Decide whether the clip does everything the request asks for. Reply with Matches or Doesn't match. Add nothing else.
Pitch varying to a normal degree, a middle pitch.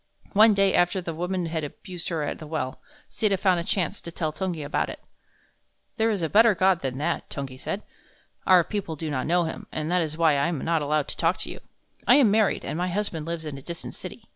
Matches